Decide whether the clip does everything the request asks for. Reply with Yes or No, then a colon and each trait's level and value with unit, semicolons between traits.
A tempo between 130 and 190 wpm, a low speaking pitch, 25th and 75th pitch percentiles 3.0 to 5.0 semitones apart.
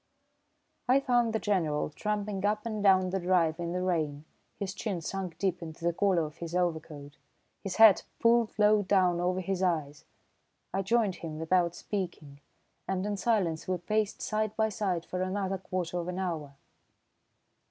No: average, 170 wpm; medium, 185 Hz; average, 3.3 semitones